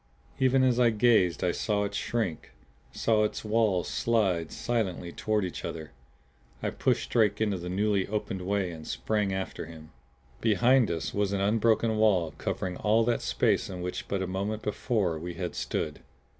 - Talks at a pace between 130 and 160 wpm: No, average, 170 wpm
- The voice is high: No, low, 100 Hz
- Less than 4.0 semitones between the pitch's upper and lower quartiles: Yes, average, 3.5 semitones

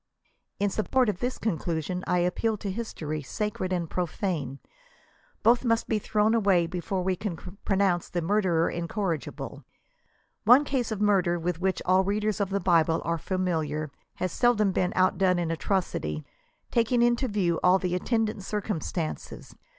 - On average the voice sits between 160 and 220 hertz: Yes, medium, 185 Hz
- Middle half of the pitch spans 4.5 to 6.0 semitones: No, average, 3.5 semitones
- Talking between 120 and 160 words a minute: Yes, average, 150 wpm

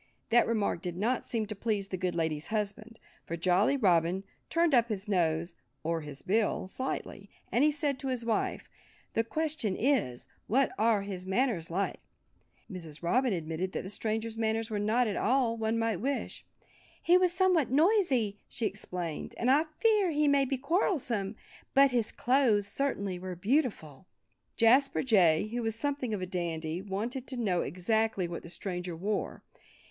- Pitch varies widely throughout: Yes, wide, 5.9 semitones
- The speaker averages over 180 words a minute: No, average, 165 wpm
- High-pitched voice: Yes, high, 220 Hz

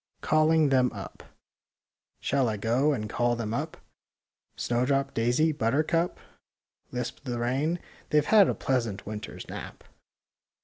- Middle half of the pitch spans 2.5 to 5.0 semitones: Yes, average, 4.5 semitones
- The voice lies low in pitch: Yes, low, 130 Hz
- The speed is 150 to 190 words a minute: No, average, 140 wpm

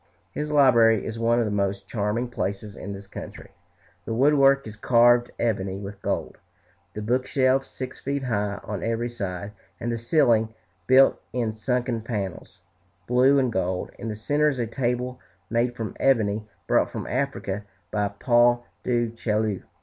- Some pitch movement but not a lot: Yes, average, 3.3 semitones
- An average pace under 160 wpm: No, average, 165 wpm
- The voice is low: Yes, low, 115 Hz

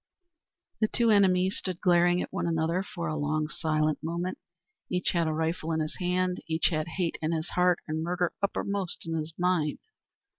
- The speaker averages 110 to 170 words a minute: No, average, 185 wpm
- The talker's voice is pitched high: No, medium, 170 Hz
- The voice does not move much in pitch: Yes, narrow, 2.3 semitones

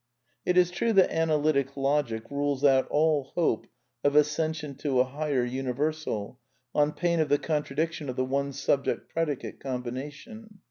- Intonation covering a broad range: No, average, 2.7 semitones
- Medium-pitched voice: Yes, medium, 145 Hz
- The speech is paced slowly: No, average, 155 wpm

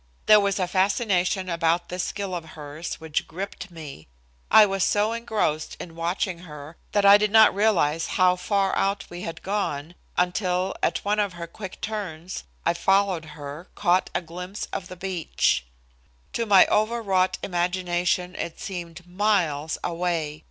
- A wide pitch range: No, average, 3.0 semitones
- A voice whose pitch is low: No, medium, 180 Hz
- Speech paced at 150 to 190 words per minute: Yes, average, 160 wpm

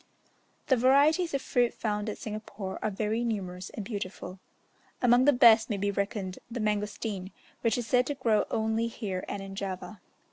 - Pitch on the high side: Yes, high, 215 Hz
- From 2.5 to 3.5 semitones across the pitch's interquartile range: Yes, average, 3.2 semitones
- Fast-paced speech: No, average, 175 wpm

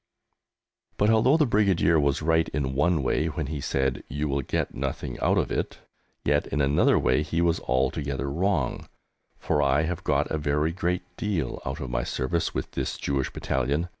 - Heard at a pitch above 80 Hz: No, very low, 75 Hz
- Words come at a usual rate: Yes, average, 185 wpm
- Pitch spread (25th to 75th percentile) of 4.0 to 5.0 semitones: No, average, 3.5 semitones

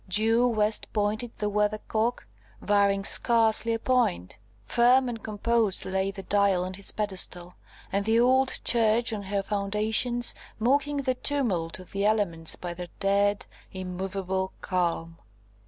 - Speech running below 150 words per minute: Yes, average, 140 wpm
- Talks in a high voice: Yes, high, 205 Hz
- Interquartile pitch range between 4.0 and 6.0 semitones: No, average, 3.4 semitones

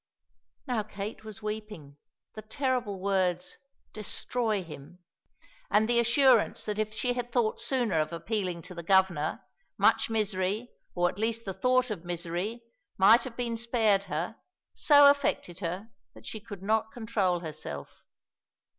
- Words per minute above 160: No, average, 145 wpm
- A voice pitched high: Yes, high, 210 Hz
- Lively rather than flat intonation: No, average, 4.4 semitones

